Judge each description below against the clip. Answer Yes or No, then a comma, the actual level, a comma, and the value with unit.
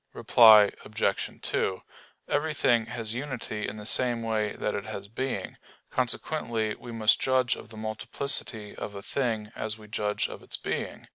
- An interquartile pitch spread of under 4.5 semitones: Yes, narrow, 2.6 semitones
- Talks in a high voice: No, low, 110 Hz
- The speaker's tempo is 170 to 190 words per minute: No, average, 160 wpm